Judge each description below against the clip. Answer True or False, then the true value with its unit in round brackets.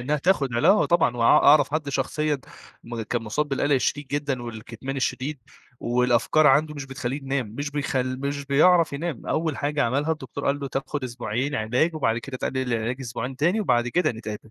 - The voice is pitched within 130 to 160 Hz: True (135 Hz)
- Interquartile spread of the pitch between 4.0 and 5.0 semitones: False (3.4 semitones)